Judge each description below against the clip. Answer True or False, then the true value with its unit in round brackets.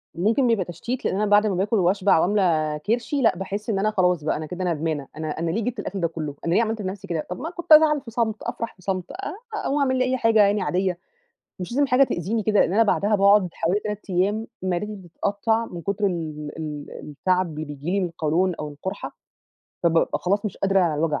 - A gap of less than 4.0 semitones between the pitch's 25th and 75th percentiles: False (4.3 semitones)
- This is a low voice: False (195 Hz)